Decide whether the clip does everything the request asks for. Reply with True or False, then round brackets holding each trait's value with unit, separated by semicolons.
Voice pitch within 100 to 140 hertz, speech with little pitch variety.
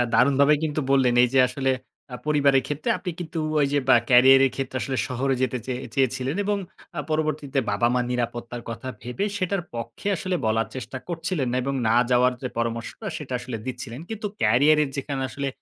False (135 Hz; 3.3 semitones)